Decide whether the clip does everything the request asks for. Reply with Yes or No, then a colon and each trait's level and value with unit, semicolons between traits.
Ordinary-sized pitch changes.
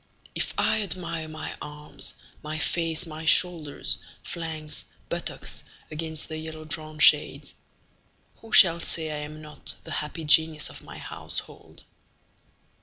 No: narrow, 1.3 semitones